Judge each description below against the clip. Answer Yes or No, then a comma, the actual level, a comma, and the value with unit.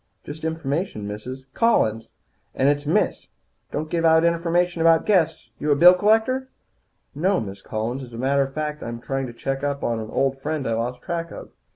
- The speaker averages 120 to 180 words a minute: No, average, 200 wpm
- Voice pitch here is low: No, medium, 145 Hz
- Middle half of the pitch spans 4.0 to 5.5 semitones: Yes, average, 4.7 semitones